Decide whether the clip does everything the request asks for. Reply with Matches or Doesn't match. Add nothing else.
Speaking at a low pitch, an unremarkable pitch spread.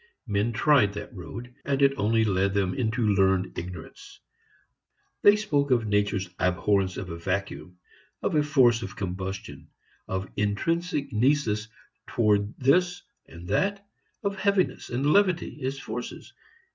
Doesn't match